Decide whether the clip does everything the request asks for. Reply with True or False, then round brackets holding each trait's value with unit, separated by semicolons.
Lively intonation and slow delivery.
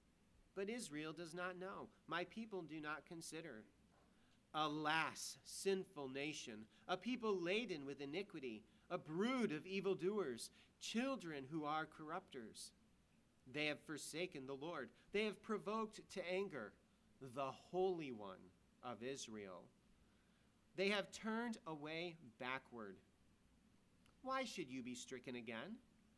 True (5.9 semitones; 120 wpm)